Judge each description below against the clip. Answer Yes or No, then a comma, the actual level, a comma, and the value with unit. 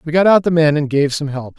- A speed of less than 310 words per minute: No, fast, 340 wpm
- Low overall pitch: No, medium, 155 Hz